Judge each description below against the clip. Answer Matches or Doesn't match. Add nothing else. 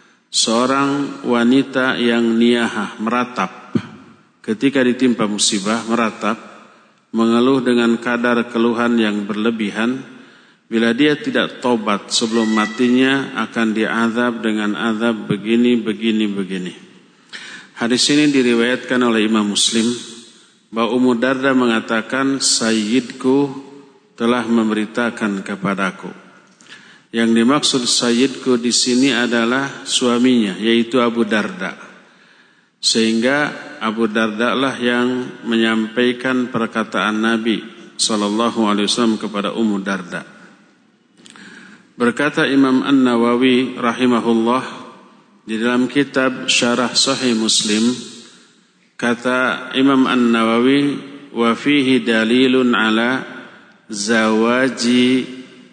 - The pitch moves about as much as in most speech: Doesn't match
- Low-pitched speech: Matches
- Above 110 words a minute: Doesn't match